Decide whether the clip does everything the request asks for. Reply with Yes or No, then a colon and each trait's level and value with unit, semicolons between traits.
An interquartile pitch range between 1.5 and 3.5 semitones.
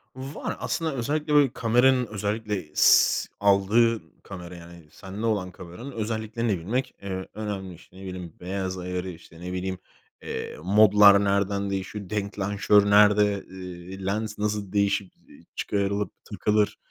Yes: narrow, 2.4 semitones